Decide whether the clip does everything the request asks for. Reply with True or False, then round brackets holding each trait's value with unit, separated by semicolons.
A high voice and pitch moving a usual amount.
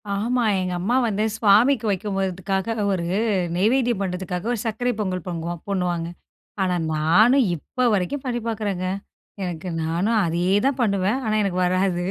True (195 Hz; 4.0 semitones)